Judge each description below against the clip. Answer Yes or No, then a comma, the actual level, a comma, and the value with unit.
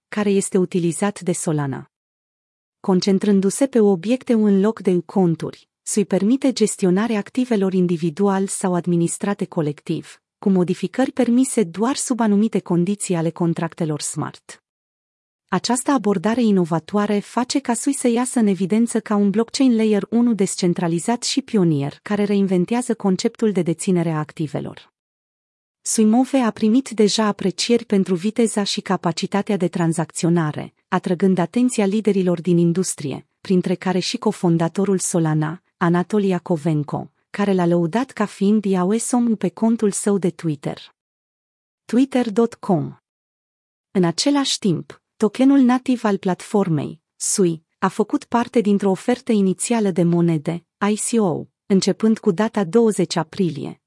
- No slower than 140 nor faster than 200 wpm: No, average, 125 wpm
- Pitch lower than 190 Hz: No, high, 200 Hz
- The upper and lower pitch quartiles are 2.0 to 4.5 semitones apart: Yes, average, 4.2 semitones